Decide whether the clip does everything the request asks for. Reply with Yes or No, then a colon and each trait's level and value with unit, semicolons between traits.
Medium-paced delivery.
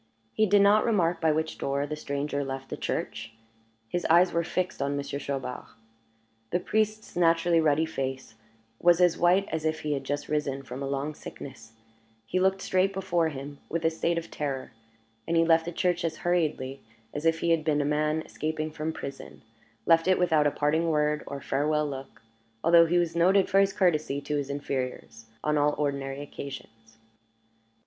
Yes: average, 190 wpm